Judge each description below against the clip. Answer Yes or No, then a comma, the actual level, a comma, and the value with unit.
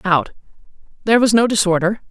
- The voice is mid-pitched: No, high, 200 Hz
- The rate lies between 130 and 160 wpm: Yes, average, 140 wpm